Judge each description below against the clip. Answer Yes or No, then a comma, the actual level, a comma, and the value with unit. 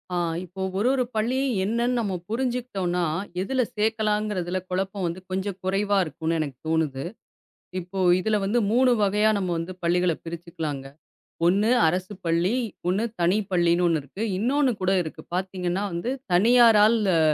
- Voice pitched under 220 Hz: Yes, high, 190 Hz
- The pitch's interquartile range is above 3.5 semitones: Yes, average, 3.9 semitones